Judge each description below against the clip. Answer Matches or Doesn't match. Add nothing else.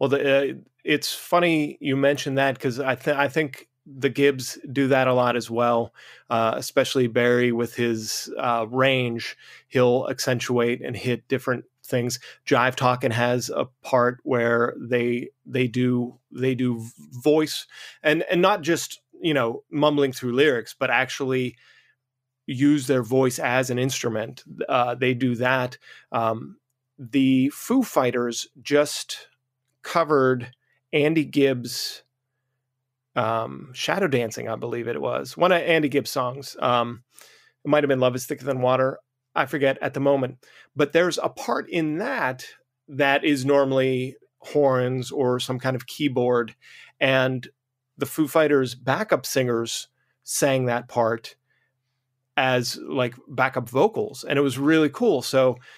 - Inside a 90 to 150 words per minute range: Matches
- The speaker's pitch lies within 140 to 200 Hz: Doesn't match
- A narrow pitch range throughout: Matches